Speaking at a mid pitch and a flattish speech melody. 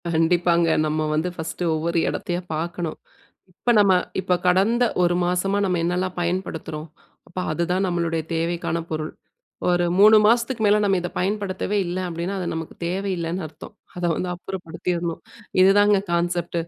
Yes: medium, 175 Hz; narrow, 2.1 semitones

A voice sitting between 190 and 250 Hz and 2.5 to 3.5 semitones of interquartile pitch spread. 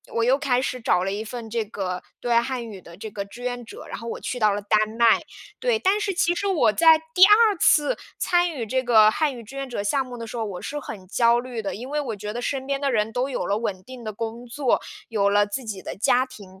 No: high, 235 Hz; average, 4.3 semitones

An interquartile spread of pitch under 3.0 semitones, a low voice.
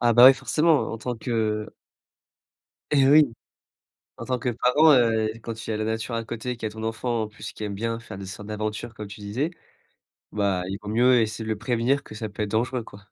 Yes: narrow, 2.5 semitones; low, 115 Hz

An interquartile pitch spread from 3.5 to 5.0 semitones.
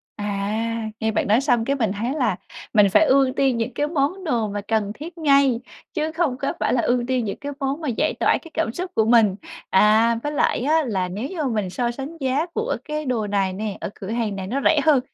No: wide, 5.4 semitones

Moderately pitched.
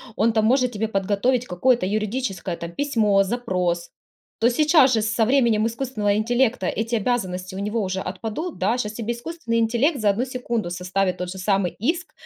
No: high, 220 Hz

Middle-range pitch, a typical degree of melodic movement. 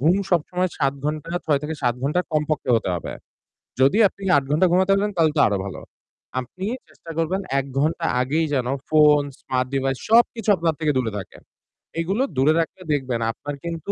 Yes: medium, 155 Hz; average, 4.6 semitones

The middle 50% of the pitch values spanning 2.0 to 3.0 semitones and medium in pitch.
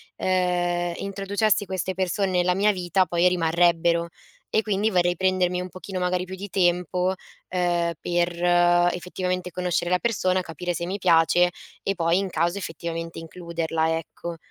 No: narrow, 1.5 semitones; medium, 180 Hz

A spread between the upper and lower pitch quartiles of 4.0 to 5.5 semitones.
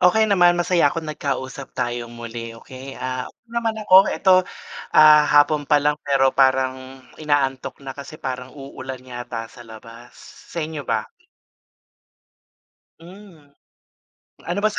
Yes: average, 4.3 semitones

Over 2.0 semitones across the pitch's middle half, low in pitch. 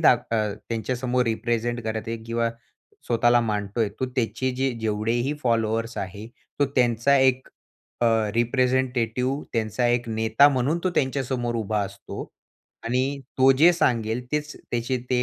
Yes: narrow, 2.4 semitones; low, 120 Hz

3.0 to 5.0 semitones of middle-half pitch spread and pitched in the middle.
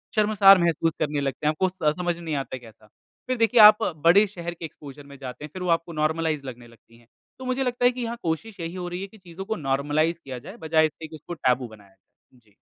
No: wide, 5.5 semitones; medium, 165 Hz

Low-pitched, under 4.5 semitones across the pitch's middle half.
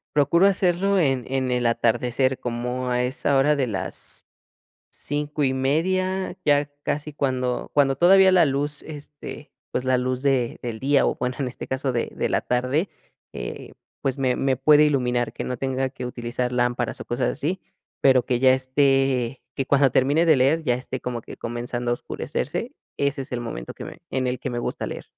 Yes: low, 130 Hz; average, 2.7 semitones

